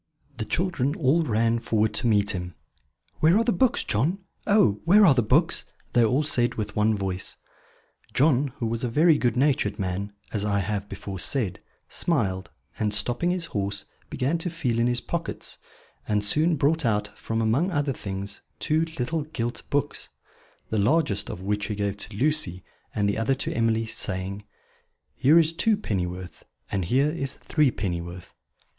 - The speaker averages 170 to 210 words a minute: Yes, average, 175 wpm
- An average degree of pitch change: No, wide, 6.8 semitones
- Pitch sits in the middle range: No, low, 115 Hz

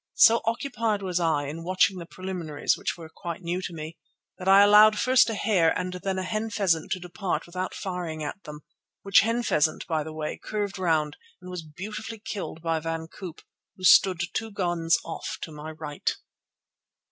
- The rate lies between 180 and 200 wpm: Yes, average, 190 wpm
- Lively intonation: No, average, 3.8 semitones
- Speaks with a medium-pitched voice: Yes, medium, 180 Hz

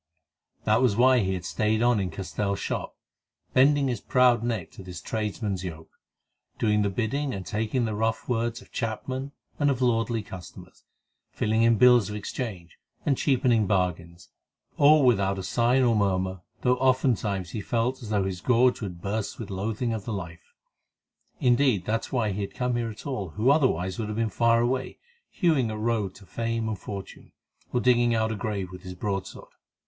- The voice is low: Yes, low, 110 Hz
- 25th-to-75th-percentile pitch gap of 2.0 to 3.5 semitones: No, average, 3.9 semitones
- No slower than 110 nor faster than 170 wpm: No, average, 185 wpm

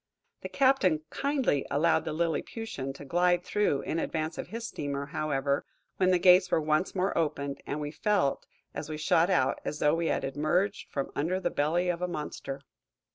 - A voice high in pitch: No, medium, 160 Hz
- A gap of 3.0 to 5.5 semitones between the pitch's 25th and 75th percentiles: Yes, average, 3.9 semitones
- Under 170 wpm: No, average, 185 wpm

